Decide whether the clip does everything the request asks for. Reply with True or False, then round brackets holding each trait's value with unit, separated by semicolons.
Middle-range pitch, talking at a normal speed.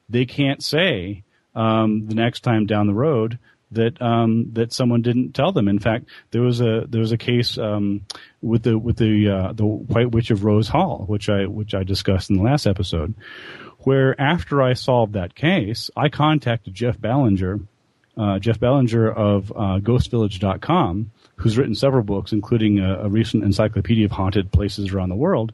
False (110 Hz; 185 wpm)